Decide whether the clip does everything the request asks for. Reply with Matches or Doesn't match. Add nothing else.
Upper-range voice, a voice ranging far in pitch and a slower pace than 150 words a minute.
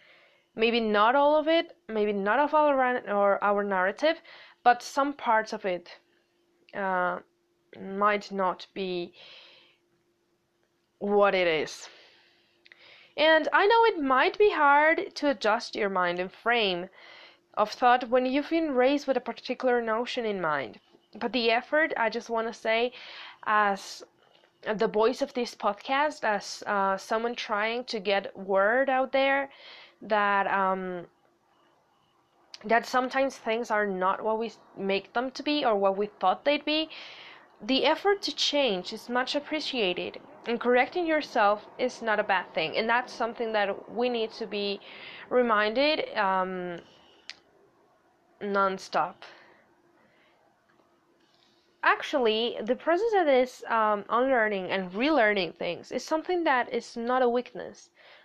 Matches